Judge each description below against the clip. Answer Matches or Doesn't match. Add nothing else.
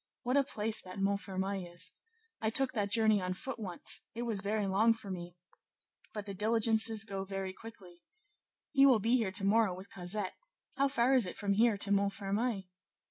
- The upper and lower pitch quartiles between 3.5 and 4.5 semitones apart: Doesn't match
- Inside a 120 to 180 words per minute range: Doesn't match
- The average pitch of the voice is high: Matches